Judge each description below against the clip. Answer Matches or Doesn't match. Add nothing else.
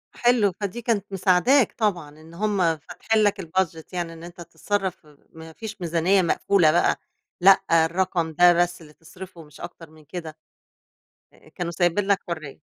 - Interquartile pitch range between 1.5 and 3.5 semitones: Matches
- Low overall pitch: Doesn't match